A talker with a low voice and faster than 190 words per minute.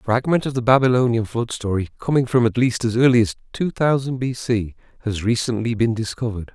Yes: low, 120 Hz; average, 200 wpm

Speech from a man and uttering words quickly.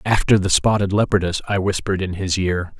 No: male; average, 195 wpm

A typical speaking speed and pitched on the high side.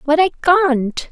Yes: average, 160 wpm; very high, 315 Hz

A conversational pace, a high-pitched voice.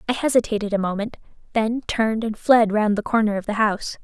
No: fast, 210 wpm; high, 220 Hz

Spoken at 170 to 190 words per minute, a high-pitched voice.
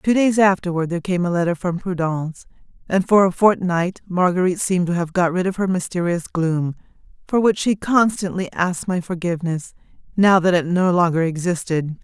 No: average, 180 wpm; medium, 180 Hz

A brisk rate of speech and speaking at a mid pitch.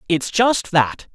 No: average, 155 wpm; medium, 180 Hz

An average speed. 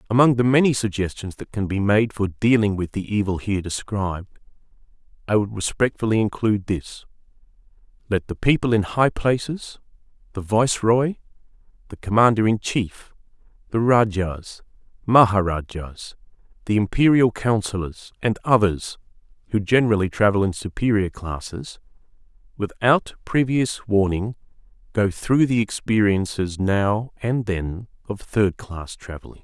No: slow, 120 wpm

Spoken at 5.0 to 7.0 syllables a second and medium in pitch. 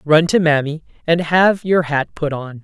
No: 4.3 syllables/s; medium, 160 Hz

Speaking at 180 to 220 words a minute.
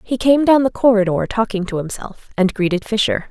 Yes: average, 200 wpm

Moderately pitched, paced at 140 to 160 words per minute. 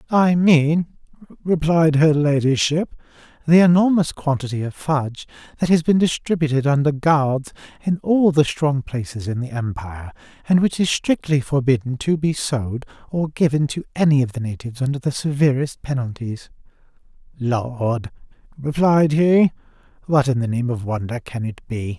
Yes: medium, 145 Hz; average, 150 wpm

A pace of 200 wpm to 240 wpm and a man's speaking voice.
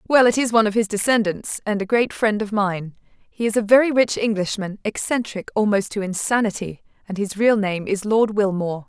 No: fast, 205 wpm; female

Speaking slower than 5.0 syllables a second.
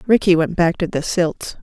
Yes: 4.8 syllables/s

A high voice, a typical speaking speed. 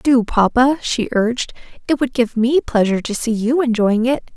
Yes: high, 240 Hz; average, 195 wpm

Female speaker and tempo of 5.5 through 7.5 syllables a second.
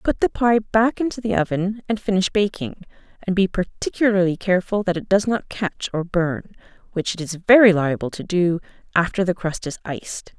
No: female; 5.1 syllables/s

